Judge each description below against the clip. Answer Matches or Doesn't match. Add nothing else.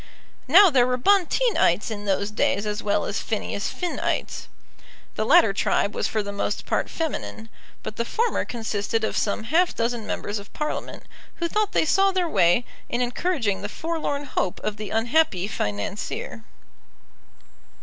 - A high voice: Matches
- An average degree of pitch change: Doesn't match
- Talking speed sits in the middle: Matches